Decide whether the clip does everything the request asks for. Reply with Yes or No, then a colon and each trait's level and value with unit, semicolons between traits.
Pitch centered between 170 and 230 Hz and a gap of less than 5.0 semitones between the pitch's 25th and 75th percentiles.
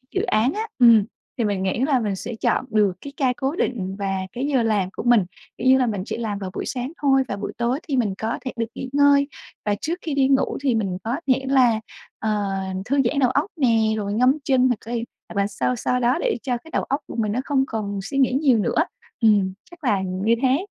No: high, 240 Hz; average, 4.2 semitones